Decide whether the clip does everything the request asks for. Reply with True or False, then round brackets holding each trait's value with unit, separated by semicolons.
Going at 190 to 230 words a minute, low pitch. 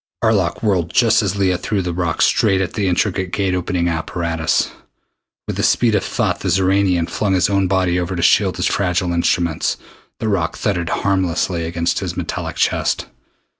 False (175 wpm; 90 Hz)